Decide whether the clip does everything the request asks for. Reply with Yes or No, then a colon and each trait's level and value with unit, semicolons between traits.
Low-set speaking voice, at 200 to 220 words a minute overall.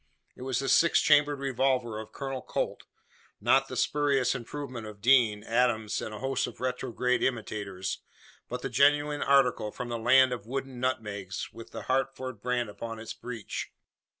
No: low, 125 Hz; average, 165 wpm